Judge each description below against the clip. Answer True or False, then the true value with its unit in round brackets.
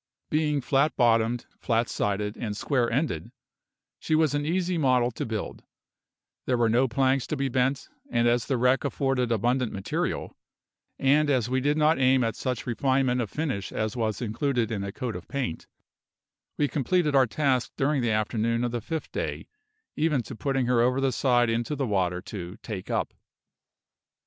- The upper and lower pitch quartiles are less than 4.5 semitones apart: True (3.2 semitones)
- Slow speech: False (180 wpm)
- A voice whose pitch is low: True (125 Hz)